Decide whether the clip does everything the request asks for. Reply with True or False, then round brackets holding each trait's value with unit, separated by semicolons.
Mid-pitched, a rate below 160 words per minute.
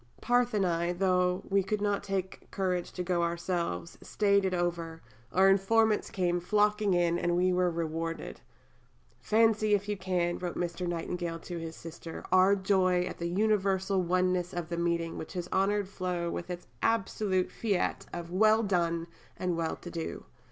False (180 Hz; 170 wpm)